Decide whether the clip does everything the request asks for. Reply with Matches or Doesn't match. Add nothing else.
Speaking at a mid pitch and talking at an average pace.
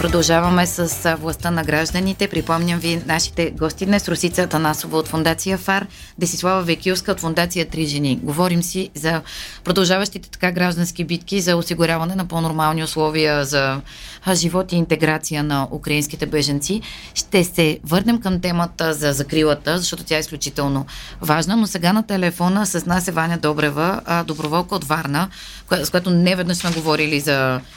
Matches